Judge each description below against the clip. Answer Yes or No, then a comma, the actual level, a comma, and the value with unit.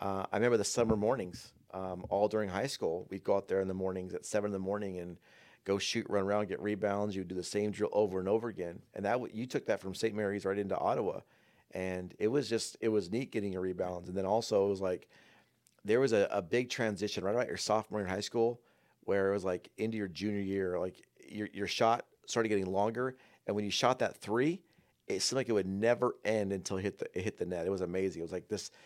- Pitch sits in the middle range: No, low, 100 Hz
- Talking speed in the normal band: No, fast, 255 wpm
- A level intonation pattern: Yes, narrow, 2.1 semitones